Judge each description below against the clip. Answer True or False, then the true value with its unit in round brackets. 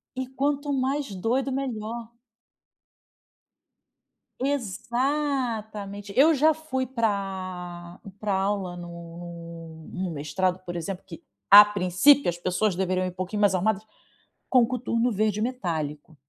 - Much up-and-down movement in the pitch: True (6.2 semitones)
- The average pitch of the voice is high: True (205 Hz)